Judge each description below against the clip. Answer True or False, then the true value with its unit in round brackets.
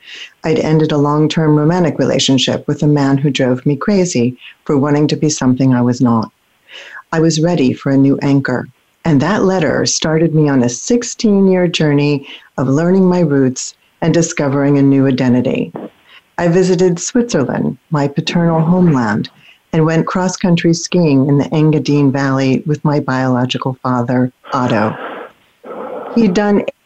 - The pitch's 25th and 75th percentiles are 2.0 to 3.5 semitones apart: False (4.1 semitones)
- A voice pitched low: False (150 Hz)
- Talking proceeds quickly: False (150 wpm)